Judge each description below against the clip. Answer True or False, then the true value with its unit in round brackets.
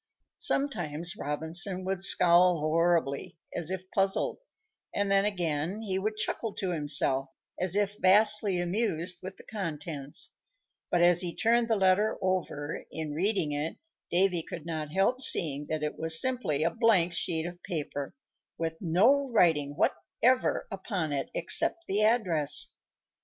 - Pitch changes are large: False (4.0 semitones)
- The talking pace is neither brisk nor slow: True (145 wpm)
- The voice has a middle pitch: True (175 Hz)